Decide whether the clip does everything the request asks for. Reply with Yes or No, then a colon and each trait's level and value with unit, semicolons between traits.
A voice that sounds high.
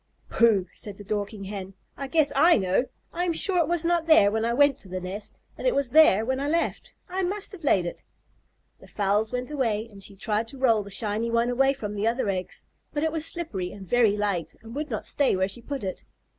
Yes: high, 230 Hz